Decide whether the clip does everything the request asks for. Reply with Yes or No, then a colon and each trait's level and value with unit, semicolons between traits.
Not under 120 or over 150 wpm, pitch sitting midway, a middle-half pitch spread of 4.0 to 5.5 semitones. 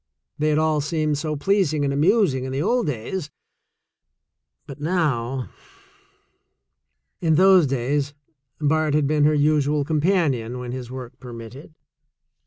No: average, 140 wpm; medium, 150 Hz; average, 3.0 semitones